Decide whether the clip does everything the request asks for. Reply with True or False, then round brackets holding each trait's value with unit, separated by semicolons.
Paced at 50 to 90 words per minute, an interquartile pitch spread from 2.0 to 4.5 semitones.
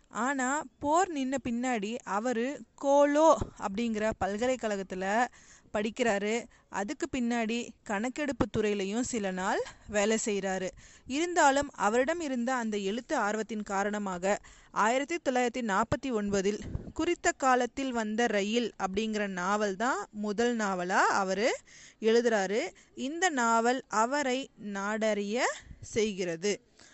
False (100 wpm; 4.2 semitones)